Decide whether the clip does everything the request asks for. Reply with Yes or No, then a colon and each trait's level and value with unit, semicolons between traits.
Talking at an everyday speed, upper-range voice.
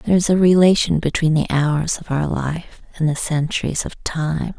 No: average, 195 wpm; medium, 160 Hz